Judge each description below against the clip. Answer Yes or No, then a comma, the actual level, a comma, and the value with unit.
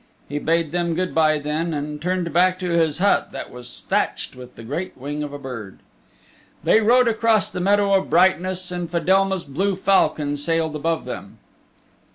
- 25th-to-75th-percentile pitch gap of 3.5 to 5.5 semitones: Yes, average, 4.1 semitones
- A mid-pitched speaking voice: Yes, medium, 170 Hz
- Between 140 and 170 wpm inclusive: No, average, 180 wpm